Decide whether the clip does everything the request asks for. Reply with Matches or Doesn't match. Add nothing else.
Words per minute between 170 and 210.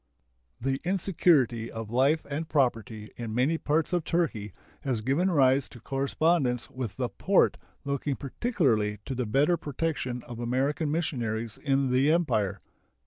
Doesn't match